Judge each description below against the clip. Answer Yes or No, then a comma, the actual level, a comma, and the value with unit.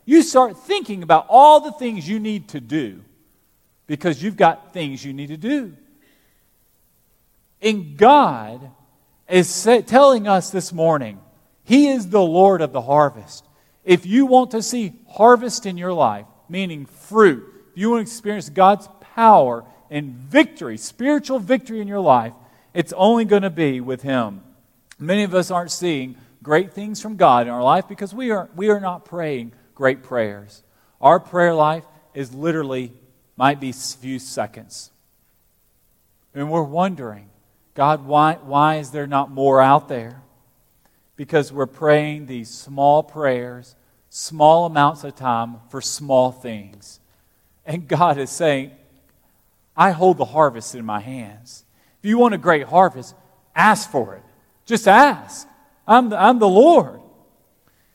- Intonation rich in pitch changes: Yes, wide, 7.4 semitones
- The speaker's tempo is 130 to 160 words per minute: Yes, average, 155 wpm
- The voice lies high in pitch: No, medium, 155 Hz